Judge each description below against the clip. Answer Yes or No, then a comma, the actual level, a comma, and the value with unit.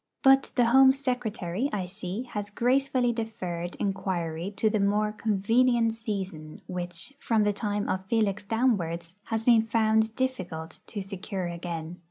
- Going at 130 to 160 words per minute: Yes, average, 145 wpm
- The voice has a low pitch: No, high, 210 Hz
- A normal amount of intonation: Yes, average, 4.1 semitones